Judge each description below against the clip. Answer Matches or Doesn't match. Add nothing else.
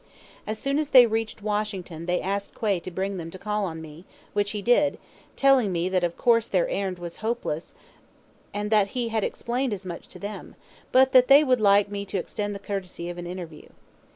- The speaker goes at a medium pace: Doesn't match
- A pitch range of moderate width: Matches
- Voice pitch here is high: Matches